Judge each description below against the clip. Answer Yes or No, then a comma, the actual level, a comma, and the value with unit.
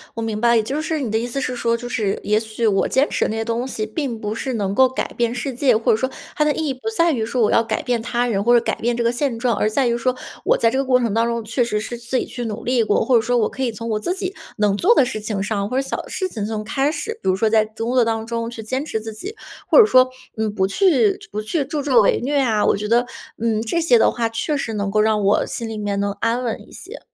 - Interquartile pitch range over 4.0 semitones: No, average, 3.0 semitones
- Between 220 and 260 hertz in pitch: Yes, high, 230 Hz